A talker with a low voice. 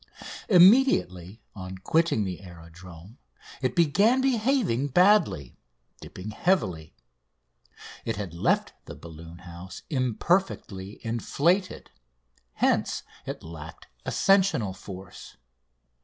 Yes: low, 105 Hz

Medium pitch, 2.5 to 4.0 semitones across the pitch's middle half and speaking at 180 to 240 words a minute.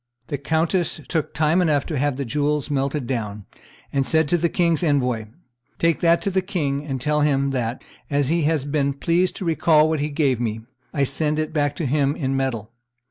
Yes: medium, 145 Hz; average, 2.9 semitones; fast, 205 wpm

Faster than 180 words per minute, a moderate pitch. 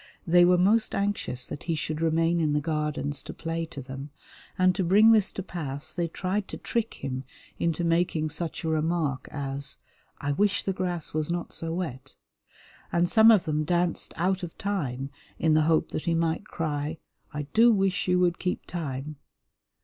Yes: average, 190 wpm; medium, 165 Hz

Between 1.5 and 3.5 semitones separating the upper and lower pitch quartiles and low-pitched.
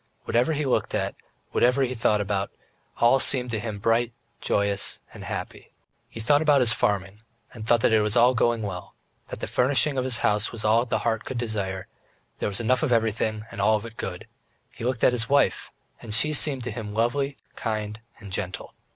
Yes: average, 3.0 semitones; low, 115 Hz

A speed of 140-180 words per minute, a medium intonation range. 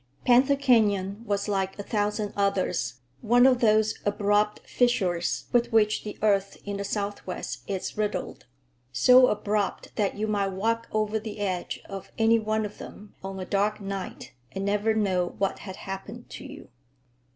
No: average, 160 wpm; narrow, 1.9 semitones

